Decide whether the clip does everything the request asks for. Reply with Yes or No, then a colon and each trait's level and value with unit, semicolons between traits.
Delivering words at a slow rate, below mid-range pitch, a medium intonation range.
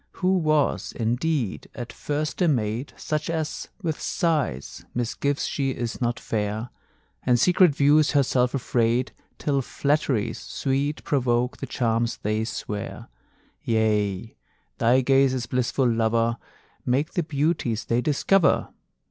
Yes: slow, 120 wpm; low, 125 Hz; average, 4.3 semitones